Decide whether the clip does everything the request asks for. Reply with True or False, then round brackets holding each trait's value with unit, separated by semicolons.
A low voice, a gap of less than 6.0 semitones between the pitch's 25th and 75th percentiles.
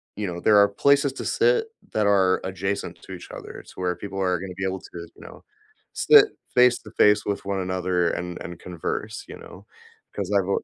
True (95 Hz; 2.4 semitones)